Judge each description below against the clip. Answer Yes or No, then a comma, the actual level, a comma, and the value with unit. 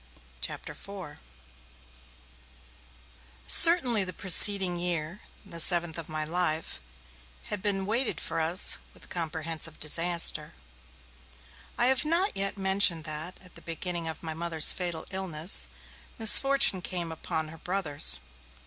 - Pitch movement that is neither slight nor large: Yes, average, 3.4 semitones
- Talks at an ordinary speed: No, slow, 120 wpm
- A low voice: No, medium, 175 Hz